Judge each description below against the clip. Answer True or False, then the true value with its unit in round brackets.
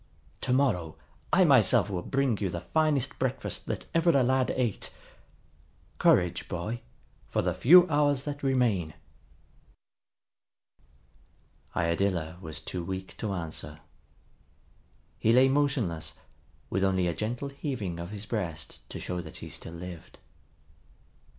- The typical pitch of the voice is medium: False (105 Hz)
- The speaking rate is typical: False (130 wpm)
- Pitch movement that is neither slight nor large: False (7.4 semitones)